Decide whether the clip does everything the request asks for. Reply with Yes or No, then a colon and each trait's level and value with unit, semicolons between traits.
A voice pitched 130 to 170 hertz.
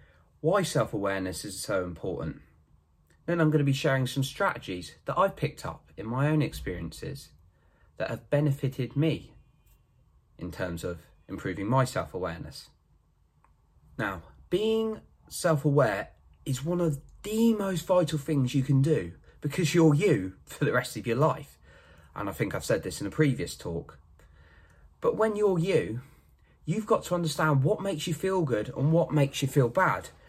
Yes: medium, 140 Hz